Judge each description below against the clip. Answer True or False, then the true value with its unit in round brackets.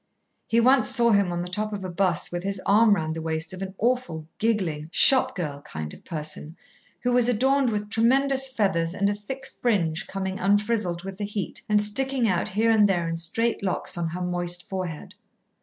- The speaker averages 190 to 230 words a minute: True (205 wpm)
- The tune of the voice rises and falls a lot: False (4.8 semitones)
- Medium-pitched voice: False (200 Hz)